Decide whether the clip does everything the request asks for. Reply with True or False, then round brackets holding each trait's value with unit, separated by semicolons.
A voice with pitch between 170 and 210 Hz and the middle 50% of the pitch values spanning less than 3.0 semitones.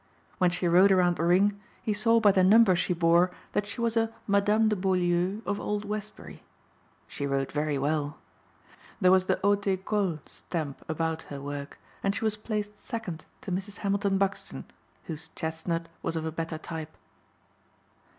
False (185 Hz; 4.1 semitones)